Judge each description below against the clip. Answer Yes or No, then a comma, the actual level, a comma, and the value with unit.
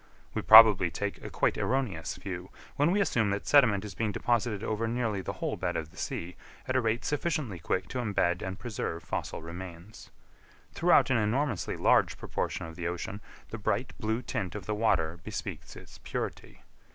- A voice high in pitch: No, low, 105 Hz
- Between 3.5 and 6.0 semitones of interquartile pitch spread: Yes, average, 4.5 semitones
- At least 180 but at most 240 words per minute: Yes, average, 185 wpm